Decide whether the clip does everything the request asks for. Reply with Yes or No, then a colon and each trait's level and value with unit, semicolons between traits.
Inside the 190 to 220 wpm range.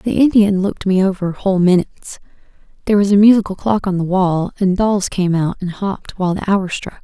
Yes: fast, 205 wpm